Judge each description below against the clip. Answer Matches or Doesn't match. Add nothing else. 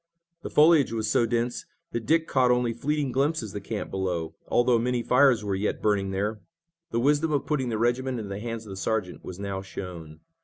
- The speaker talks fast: Matches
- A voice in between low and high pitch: Doesn't match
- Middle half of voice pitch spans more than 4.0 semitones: Matches